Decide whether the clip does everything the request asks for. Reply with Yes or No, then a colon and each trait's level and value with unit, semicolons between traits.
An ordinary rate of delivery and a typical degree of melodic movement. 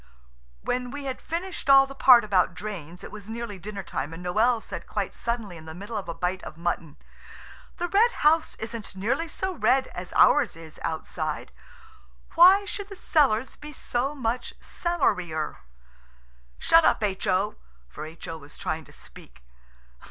No: average, 165 wpm; wide, 7.6 semitones